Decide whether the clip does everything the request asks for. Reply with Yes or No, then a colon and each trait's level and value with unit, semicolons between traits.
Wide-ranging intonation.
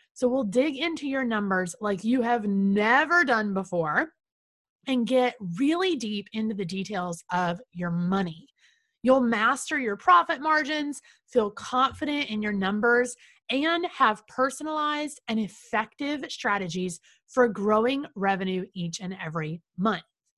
Yes: wide, 6.4 semitones